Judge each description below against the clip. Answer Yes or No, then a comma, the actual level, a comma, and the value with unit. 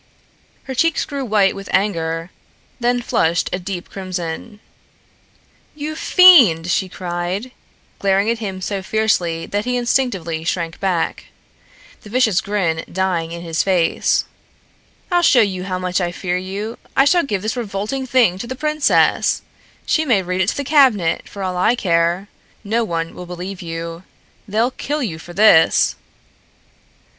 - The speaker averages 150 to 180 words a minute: Yes, average, 155 wpm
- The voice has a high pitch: Yes, high, 195 Hz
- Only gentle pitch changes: No, average, 5.2 semitones